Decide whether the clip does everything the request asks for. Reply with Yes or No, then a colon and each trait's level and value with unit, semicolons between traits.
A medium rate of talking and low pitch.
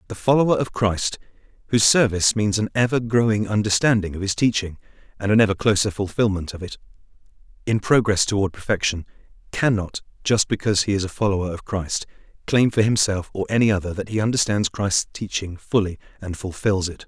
Yes: average, 170 wpm; low, 105 Hz